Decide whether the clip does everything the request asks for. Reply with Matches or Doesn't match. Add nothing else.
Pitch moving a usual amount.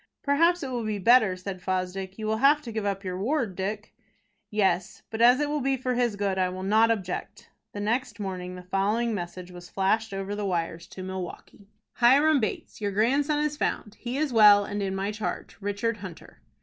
Matches